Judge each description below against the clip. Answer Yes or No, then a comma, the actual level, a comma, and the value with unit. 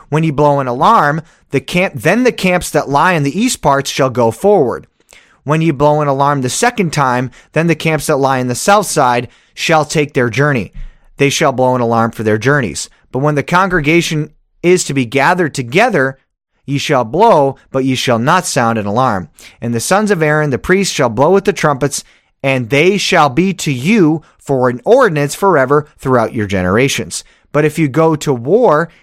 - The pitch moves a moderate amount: Yes, average, 4.0 semitones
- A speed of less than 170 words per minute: No, fast, 205 wpm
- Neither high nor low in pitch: Yes, medium, 145 Hz